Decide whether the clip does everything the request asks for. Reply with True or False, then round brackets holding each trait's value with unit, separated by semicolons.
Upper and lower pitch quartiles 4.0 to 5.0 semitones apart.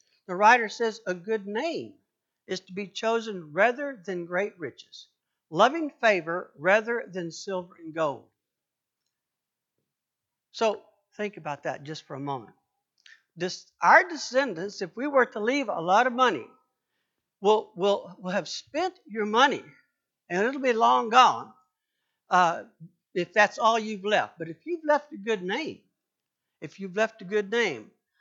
True (4.6 semitones)